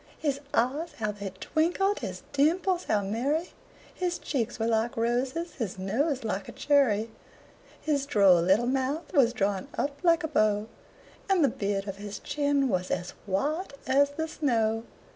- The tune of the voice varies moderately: No, wide, 6.4 semitones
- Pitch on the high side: Yes, very high, 255 Hz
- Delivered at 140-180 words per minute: Yes, average, 160 wpm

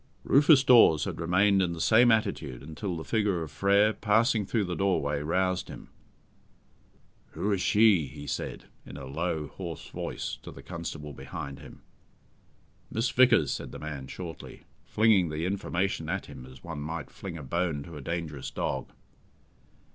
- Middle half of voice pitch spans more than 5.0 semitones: Yes, wide, 5.4 semitones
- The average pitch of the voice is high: No, very low, 85 Hz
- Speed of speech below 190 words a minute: Yes, average, 165 wpm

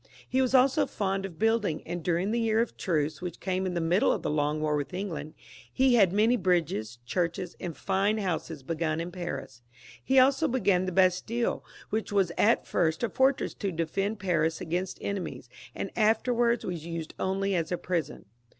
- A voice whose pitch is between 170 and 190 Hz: Yes, medium, 185 Hz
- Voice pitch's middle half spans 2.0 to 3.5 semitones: No, average, 4.7 semitones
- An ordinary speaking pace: Yes, average, 195 wpm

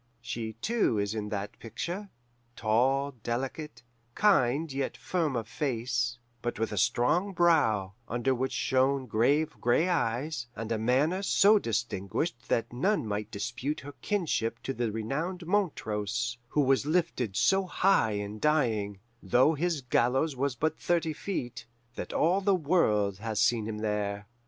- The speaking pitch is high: No, low, 125 Hz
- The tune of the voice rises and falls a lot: Yes, wide, 6.0 semitones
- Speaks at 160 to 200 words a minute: No, average, 150 wpm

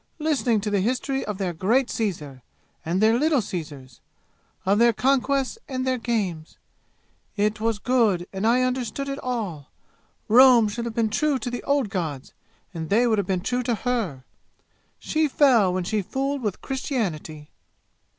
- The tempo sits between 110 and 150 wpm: No, average, 165 wpm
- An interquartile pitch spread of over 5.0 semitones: Yes, wide, 5.4 semitones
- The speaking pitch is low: No, high, 225 Hz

